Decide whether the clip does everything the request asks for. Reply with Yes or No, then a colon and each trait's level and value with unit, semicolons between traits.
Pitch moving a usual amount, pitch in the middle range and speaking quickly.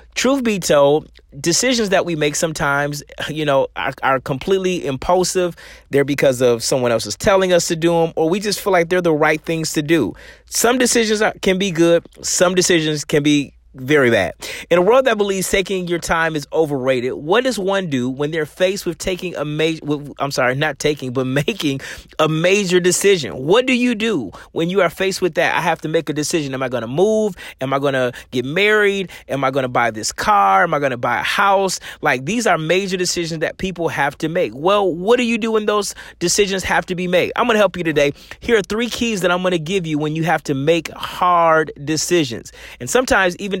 Yes: average, 4.7 semitones; medium, 170 Hz; fast, 230 wpm